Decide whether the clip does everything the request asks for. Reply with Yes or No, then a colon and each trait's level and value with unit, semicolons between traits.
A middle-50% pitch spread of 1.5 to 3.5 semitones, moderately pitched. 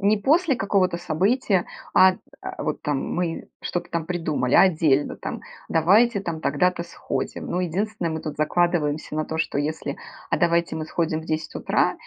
Yes: average, 3.0 semitones; medium, 170 Hz